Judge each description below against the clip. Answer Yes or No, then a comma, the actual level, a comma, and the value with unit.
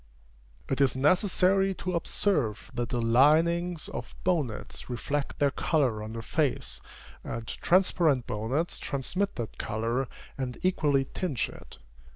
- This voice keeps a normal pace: No, slow, 130 wpm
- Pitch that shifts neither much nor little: No, wide, 6.3 semitones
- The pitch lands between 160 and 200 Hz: No, medium, 140 Hz